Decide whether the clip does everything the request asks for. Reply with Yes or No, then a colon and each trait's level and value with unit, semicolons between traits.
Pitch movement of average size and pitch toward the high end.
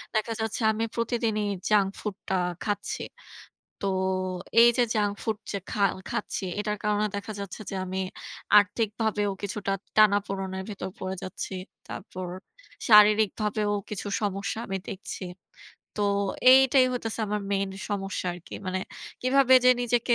No: narrow, 2.0 semitones; high, 210 Hz